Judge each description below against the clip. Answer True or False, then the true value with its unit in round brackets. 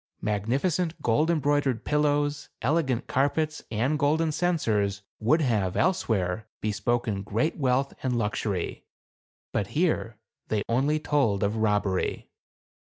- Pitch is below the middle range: True (125 Hz)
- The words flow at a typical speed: False (115 wpm)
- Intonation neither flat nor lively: False (5.9 semitones)